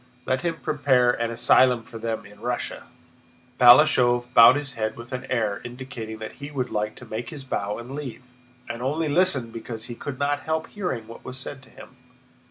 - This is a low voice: Yes, low, 125 Hz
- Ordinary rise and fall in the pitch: Yes, average, 3.3 semitones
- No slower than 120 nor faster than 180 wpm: No, average, 195 wpm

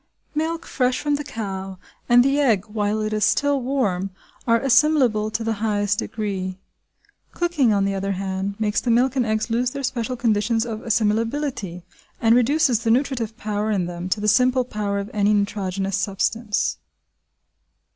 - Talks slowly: No, average, 165 wpm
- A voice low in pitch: No, high, 220 Hz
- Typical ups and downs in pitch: Yes, average, 3.8 semitones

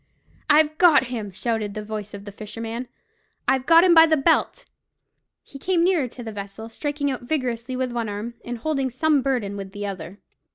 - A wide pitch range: Yes, wide, 5.8 semitones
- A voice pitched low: No, high, 245 Hz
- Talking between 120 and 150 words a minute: No, average, 195 wpm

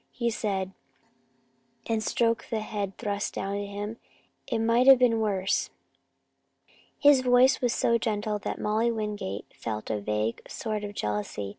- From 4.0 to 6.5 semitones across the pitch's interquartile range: No, average, 3.0 semitones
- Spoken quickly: No, average, 150 wpm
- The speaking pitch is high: Yes, high, 210 Hz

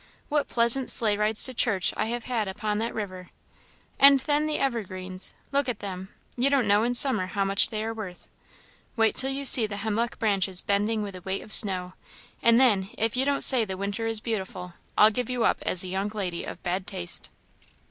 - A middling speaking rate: No, fast, 210 wpm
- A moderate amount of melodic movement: Yes, average, 3.8 semitones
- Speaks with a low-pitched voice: No, high, 215 Hz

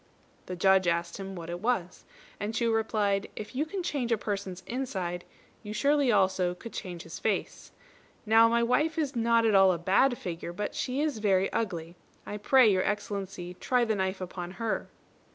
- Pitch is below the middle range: No, high, 205 Hz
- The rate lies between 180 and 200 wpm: Yes, average, 190 wpm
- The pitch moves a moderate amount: Yes, average, 4.1 semitones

